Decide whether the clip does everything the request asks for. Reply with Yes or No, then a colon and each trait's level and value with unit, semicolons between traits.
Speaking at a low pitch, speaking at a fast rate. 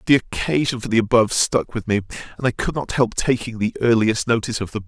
Yes: low, 115 Hz; fast, 235 wpm